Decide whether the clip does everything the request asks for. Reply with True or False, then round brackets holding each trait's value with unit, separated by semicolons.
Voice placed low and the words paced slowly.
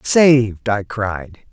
True (115 Hz; 120 wpm)